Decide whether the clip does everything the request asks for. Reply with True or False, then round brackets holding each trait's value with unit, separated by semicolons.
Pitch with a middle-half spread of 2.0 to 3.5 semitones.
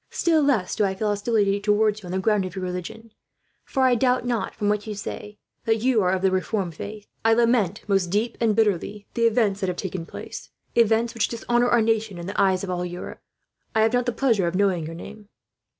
True (3.2 semitones)